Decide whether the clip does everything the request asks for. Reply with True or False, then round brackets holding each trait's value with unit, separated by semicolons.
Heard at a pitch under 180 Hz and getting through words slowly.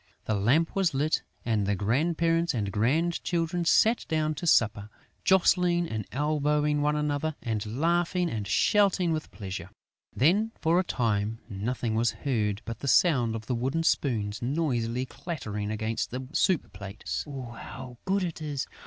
False (135 Hz; 155 wpm)